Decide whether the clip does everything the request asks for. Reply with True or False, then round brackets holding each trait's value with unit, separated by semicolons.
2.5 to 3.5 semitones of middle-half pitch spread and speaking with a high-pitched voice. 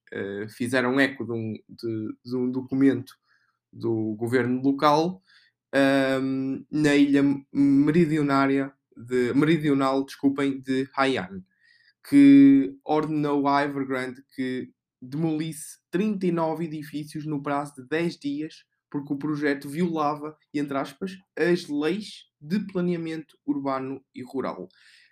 False (3.0 semitones; 140 Hz)